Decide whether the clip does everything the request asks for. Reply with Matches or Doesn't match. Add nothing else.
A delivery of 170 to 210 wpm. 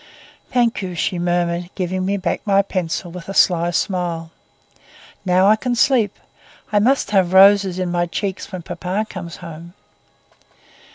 Doesn't match